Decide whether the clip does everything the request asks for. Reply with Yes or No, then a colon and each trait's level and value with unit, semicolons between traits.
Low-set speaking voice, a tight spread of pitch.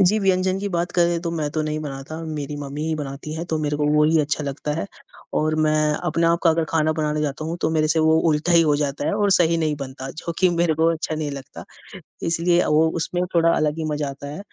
No: medium, 155 Hz; narrow, 2.0 semitones